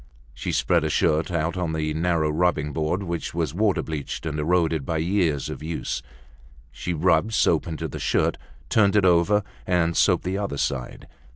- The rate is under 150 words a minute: No, average, 180 wpm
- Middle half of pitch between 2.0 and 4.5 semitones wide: Yes, narrow, 2.6 semitones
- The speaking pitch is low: Yes, very low, 85 Hz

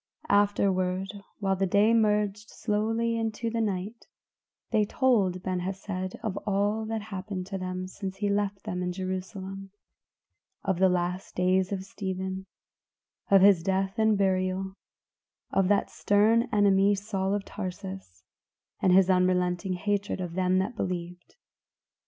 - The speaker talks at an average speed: Yes, average, 145 wpm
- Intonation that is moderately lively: No, narrow, 1.8 semitones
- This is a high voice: Yes, high, 195 Hz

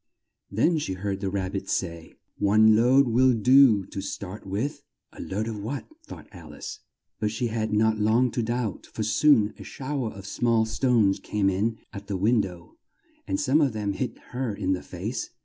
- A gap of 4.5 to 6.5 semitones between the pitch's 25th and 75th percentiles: No, average, 3.8 semitones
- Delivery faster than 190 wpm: Yes, average, 200 wpm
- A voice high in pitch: No, low, 110 Hz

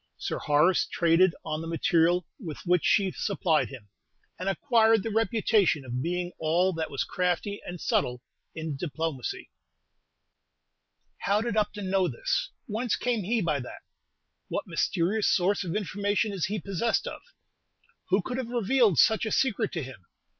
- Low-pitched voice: No, medium, 185 Hz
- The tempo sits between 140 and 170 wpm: Yes, average, 155 wpm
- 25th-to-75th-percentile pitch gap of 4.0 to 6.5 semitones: Yes, average, 4.5 semitones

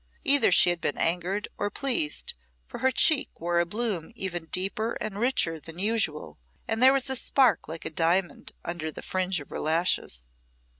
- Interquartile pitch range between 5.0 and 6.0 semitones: Yes, wide, 5.5 semitones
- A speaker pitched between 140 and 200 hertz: Yes, medium, 185 Hz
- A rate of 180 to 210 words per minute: Yes, average, 185 wpm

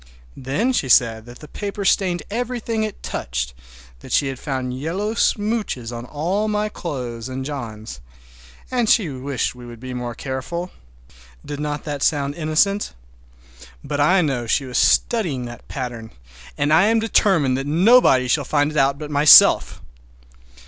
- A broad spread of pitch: Yes, wide, 7.1 semitones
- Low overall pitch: No, medium, 145 Hz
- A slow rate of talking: No, average, 160 wpm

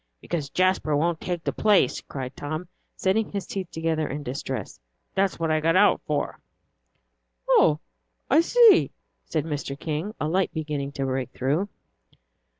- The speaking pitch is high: No, medium, 160 Hz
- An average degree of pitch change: Yes, average, 4.3 semitones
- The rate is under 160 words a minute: Yes, average, 150 wpm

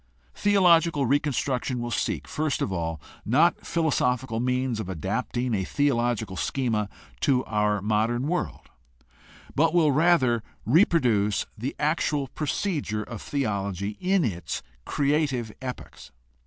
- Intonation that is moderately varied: No, wide, 5.7 semitones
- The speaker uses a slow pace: Yes, slow, 120 wpm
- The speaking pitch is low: Yes, low, 125 Hz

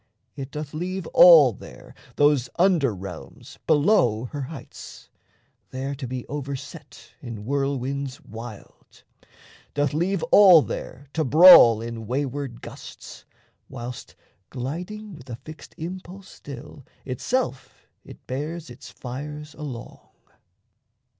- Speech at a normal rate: No, slow, 115 wpm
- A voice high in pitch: No, medium, 140 Hz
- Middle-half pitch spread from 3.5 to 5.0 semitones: Yes, average, 4.0 semitones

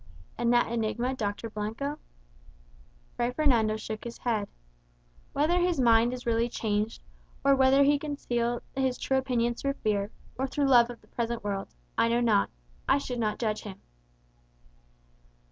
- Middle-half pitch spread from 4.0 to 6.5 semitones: No, average, 3.2 semitones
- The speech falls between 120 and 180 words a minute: Yes, average, 155 wpm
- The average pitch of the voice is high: Yes, high, 240 Hz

